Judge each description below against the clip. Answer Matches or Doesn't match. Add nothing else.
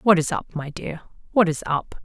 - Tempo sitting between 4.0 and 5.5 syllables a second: Matches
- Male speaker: Doesn't match